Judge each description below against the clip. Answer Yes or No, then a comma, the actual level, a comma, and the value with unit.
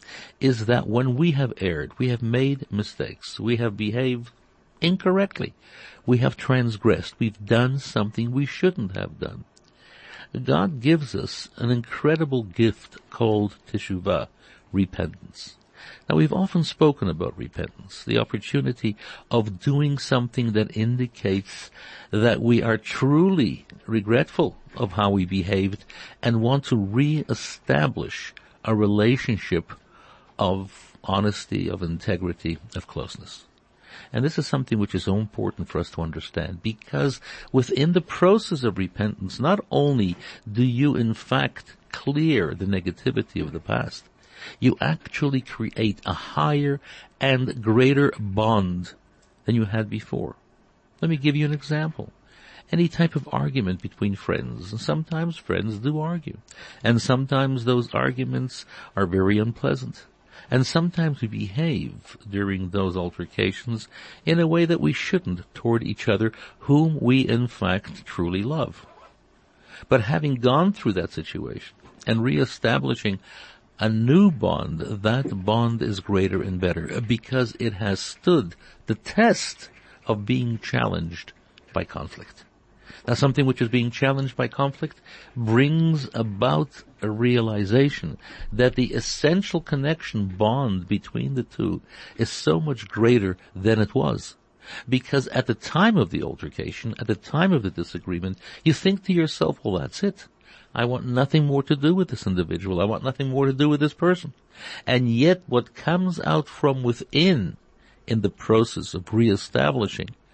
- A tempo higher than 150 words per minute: No, average, 140 wpm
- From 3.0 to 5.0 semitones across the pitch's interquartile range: No, wide, 5.6 semitones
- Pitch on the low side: Yes, low, 120 Hz